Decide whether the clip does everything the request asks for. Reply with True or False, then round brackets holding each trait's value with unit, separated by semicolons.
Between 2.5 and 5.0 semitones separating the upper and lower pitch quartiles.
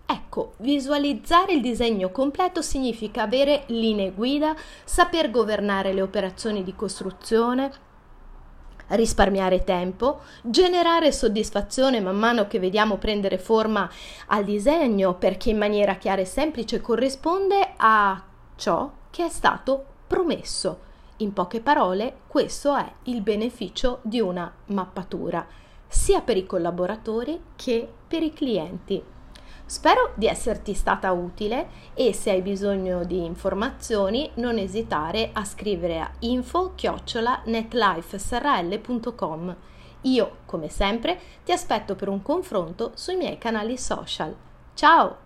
False (5.4 semitones)